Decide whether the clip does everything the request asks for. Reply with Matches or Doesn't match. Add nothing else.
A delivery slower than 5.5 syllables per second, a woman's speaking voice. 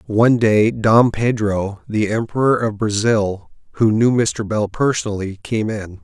Doesn't match